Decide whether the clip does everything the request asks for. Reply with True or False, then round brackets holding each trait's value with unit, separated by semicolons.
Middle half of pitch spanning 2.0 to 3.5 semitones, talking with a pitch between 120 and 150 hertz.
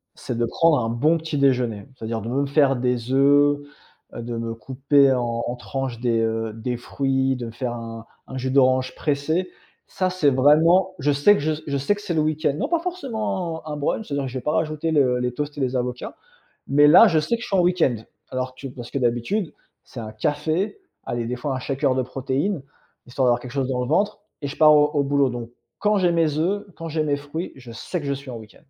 False (3.9 semitones; 140 Hz)